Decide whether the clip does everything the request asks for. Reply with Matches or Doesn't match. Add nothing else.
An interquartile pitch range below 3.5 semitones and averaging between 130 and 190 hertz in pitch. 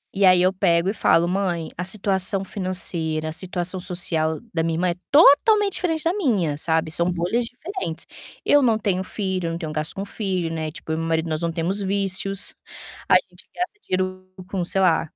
Matches